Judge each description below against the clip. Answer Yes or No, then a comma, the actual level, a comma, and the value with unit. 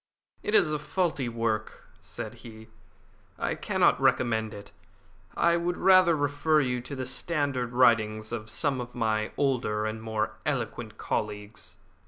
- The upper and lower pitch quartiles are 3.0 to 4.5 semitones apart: No, average, 4.9 semitones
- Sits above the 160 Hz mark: No, low, 120 Hz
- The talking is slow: No, average, 145 wpm